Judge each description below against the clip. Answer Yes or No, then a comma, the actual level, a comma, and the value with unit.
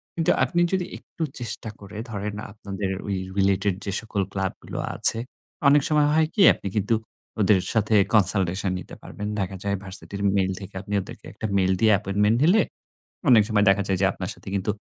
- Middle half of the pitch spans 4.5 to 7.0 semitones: No, narrow, 2.4 semitones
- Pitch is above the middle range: No, low, 100 Hz